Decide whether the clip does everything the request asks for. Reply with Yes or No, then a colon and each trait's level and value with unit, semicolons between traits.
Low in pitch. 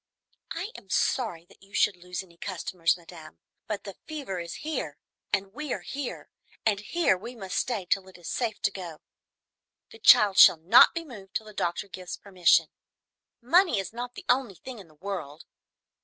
No: high, 195 Hz